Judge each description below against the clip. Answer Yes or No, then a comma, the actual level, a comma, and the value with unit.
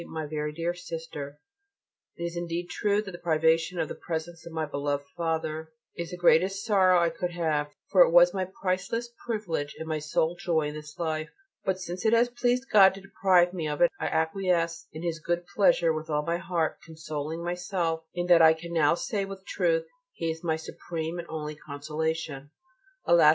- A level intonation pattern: Yes, narrow, 2.2 semitones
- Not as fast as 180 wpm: No, average, 200 wpm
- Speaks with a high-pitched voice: No, medium, 170 Hz